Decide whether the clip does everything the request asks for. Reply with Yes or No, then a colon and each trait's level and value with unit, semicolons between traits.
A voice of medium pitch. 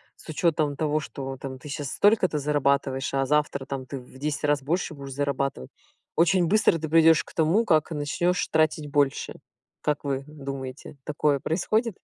Yes: medium, 145 Hz